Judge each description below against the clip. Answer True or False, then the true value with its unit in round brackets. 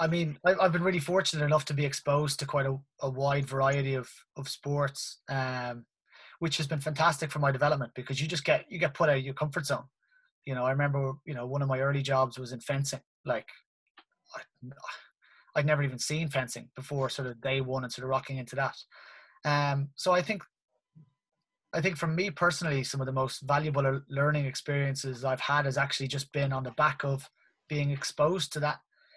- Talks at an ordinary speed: False (210 wpm)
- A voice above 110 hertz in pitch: True (140 Hz)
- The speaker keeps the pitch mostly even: True (2.2 semitones)